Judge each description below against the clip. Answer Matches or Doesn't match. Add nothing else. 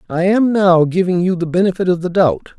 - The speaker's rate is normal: Doesn't match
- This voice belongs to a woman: Doesn't match